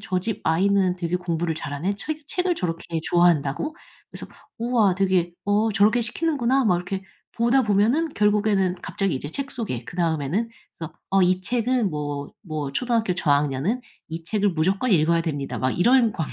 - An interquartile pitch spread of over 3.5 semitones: Yes, wide, 5.6 semitones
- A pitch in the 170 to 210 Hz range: Yes, high, 190 Hz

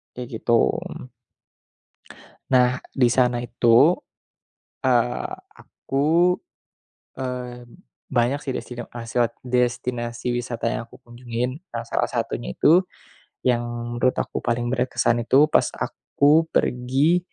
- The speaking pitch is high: No, low, 125 Hz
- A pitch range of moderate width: No, narrow, 1.9 semitones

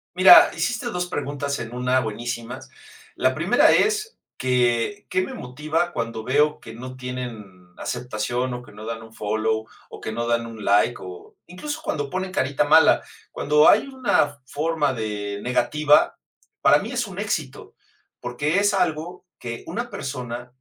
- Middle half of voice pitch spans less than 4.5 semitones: No, average, 5.0 semitones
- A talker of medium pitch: No, low, 125 Hz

